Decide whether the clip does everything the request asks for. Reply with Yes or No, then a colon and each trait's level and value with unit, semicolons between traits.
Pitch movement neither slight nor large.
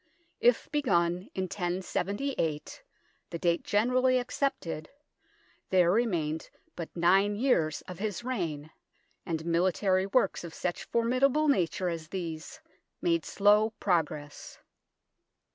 No: wide, 5.8 semitones